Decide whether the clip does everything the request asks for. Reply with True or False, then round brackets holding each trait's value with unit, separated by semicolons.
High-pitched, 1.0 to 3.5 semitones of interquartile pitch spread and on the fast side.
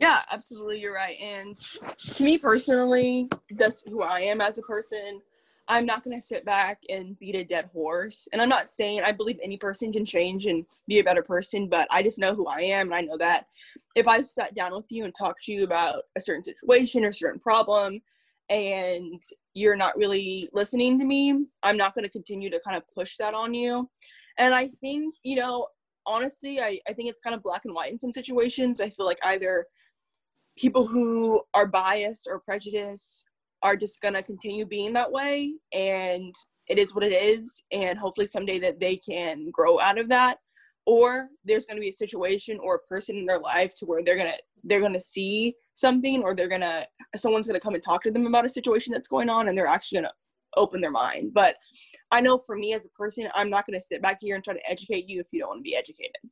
False (210 Hz; 4.3 semitones; 230 wpm)